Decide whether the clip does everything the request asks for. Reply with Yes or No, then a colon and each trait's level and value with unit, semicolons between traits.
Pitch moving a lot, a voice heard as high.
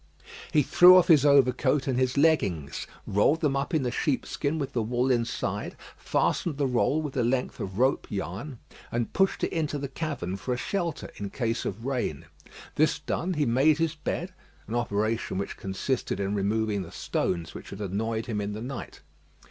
No: wide, 5.8 semitones; low, 125 Hz